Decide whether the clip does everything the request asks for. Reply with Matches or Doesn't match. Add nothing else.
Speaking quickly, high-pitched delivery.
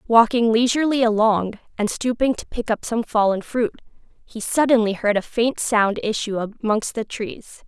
Doesn't match